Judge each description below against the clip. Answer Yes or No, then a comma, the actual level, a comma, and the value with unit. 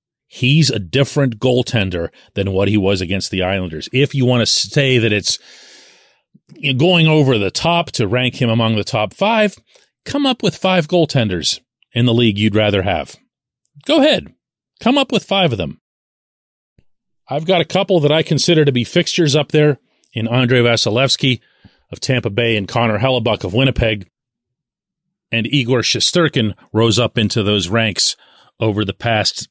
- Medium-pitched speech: No, low, 125 Hz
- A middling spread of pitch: No, wide, 5.9 semitones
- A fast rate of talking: No, average, 165 wpm